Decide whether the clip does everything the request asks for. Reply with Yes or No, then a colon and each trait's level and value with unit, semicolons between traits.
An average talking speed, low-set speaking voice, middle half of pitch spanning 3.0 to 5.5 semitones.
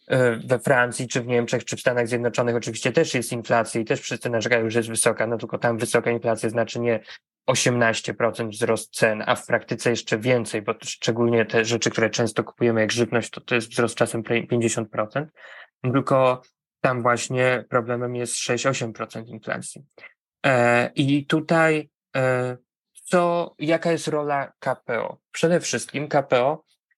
No: average, 145 wpm; low, 120 Hz; narrow, 2.4 semitones